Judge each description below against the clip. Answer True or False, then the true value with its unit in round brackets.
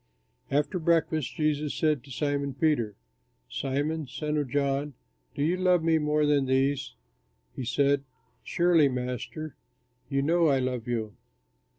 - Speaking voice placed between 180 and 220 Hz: False (145 Hz)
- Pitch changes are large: False (2.7 semitones)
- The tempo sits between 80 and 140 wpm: True (135 wpm)